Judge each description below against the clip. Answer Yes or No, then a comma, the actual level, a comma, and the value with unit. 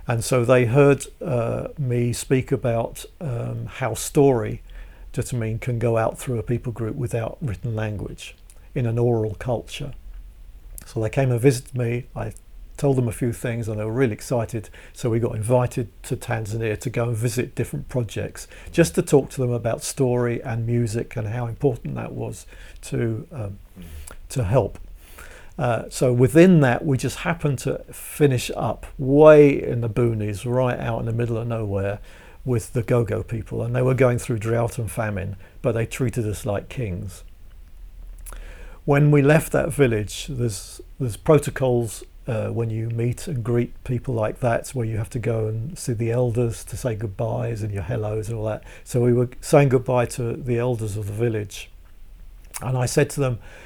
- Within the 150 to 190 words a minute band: Yes, average, 185 wpm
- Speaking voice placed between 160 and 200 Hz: No, low, 120 Hz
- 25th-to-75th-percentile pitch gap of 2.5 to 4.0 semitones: Yes, average, 2.9 semitones